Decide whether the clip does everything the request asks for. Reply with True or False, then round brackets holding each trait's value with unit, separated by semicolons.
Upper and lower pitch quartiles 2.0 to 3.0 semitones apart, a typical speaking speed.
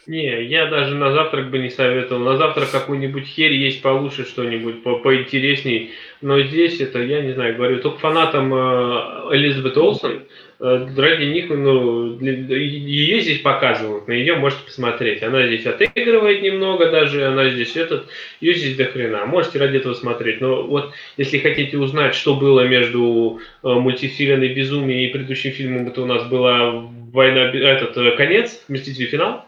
False (2.4 semitones; 165 wpm)